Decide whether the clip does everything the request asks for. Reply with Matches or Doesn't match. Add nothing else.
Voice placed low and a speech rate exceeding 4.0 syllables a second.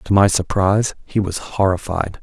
Matches